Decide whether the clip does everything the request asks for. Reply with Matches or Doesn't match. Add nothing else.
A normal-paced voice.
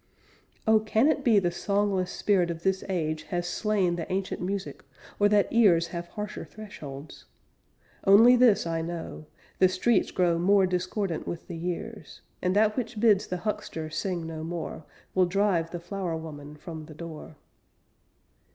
Matches